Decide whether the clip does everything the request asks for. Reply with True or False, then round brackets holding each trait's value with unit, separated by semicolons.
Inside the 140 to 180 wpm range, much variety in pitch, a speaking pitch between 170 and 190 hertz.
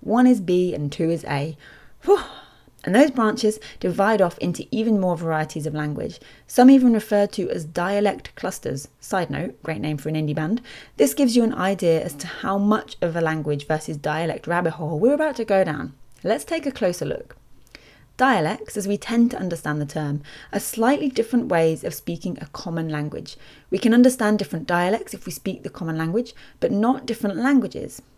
False (195 wpm; 6.6 semitones; 185 Hz)